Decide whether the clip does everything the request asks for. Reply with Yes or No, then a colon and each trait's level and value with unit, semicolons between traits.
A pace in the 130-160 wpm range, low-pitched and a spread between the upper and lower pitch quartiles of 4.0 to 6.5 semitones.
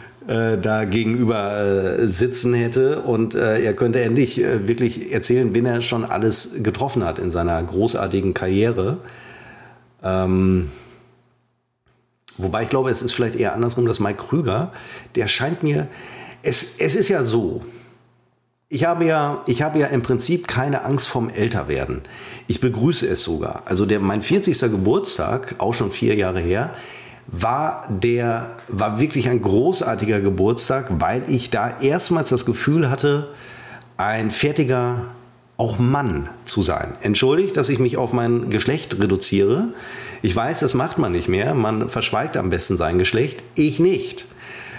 No: average, 155 wpm; low, 120 Hz; average, 3.0 semitones